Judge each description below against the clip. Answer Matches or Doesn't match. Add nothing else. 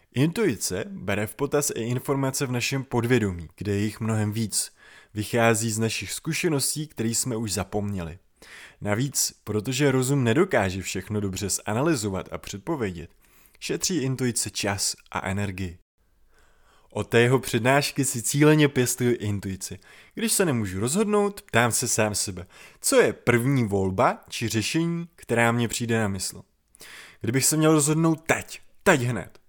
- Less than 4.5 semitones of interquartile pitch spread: Doesn't match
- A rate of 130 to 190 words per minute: Matches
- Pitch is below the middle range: Matches